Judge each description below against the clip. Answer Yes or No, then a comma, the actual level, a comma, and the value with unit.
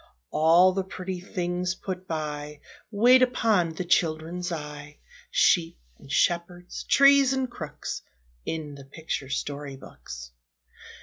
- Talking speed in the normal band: No, slow, 120 wpm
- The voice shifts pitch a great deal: No, average, 3.9 semitones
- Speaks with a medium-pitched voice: Yes, medium, 175 Hz